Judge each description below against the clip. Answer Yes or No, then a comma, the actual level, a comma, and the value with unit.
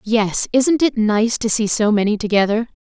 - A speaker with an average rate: Yes, average, 190 wpm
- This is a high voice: Yes, high, 220 Hz